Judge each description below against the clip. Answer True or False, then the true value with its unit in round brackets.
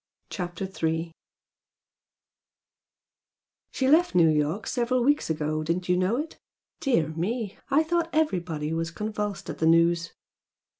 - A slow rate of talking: True (130 wpm)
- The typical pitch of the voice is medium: True (180 Hz)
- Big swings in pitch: True (7.1 semitones)